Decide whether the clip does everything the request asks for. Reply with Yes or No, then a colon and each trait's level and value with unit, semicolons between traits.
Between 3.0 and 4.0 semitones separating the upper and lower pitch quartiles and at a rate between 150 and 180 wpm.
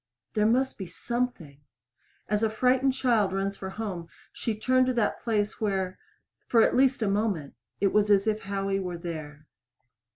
Yes: average, 3.6 semitones; average, 170 wpm